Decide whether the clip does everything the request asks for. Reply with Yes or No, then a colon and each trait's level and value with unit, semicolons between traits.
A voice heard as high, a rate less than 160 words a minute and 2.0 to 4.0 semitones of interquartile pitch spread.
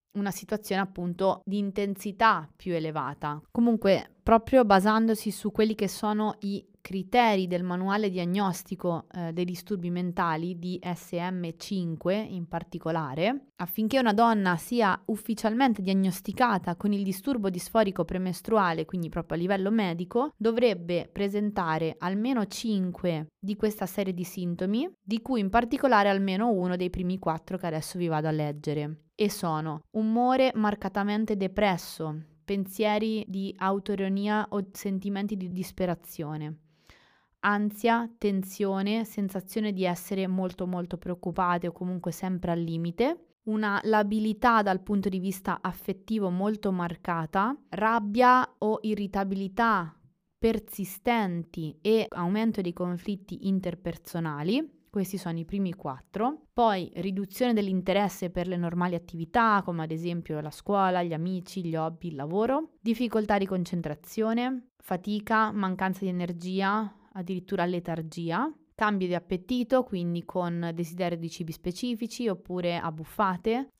Yes: high, 195 Hz; average, 125 wpm; average, 3.4 semitones